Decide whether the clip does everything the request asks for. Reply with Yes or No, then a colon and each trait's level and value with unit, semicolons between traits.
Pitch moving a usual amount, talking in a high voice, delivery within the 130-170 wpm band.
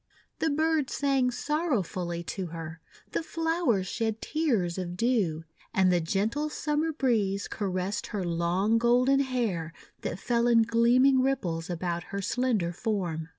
No: wide, 6.7 semitones; high, 220 Hz; average, 145 wpm